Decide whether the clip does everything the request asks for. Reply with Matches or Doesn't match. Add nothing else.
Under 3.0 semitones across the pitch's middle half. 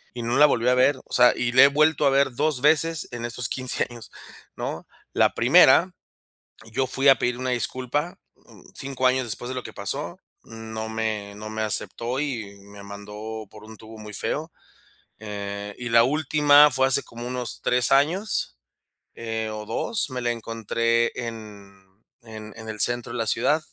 Doesn't match